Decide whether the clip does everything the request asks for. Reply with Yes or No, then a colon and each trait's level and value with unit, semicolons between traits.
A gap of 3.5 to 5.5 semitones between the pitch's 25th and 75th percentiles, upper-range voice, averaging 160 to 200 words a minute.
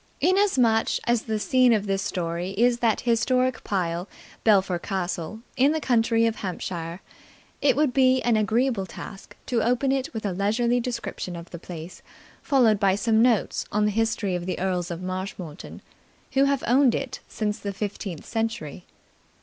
Yes: average, 4.5 semitones; high, 220 Hz; average, 165 wpm